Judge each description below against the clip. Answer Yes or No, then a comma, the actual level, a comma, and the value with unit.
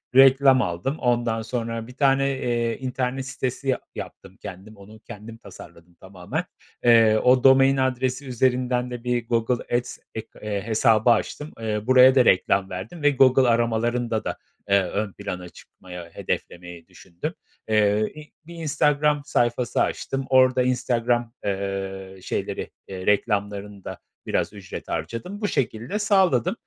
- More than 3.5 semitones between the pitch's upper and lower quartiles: Yes, average, 4.2 semitones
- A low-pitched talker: Yes, low, 120 Hz